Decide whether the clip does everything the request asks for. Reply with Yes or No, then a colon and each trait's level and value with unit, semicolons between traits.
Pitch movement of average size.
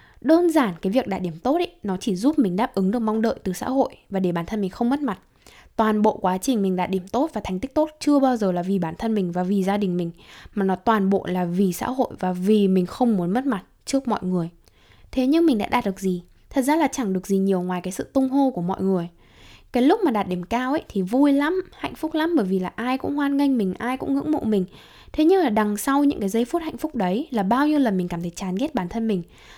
No: wide, 6.5 semitones